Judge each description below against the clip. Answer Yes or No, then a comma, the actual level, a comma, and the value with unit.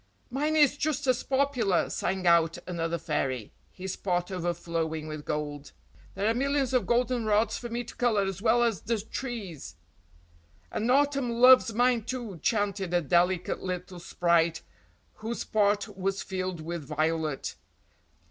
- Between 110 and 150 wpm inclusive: Yes, average, 145 wpm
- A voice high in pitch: Yes, high, 195 Hz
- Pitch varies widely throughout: Yes, wide, 6.0 semitones